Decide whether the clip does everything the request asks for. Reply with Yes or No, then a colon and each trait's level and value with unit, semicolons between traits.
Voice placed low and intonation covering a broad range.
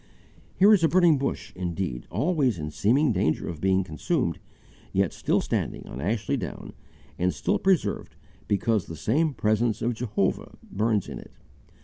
Yes: low, 110 Hz; wide, 7.4 semitones